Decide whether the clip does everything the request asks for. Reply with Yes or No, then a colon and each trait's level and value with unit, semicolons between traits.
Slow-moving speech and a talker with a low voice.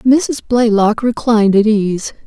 No: slow, 130 wpm; high, 225 Hz